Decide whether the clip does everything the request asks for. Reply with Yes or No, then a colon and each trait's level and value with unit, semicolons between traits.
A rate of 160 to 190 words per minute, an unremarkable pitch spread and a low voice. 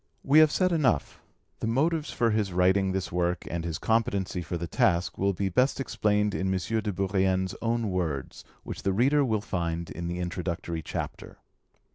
Yes: average, 180 wpm; average, 4.4 semitones; very low, 95 Hz